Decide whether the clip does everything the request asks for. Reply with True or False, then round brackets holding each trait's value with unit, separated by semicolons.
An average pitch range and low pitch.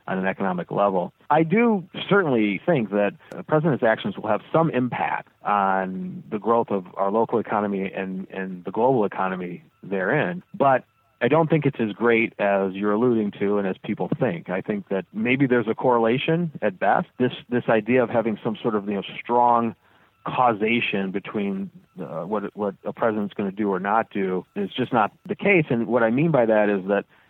False (5.9 semitones; 115 Hz)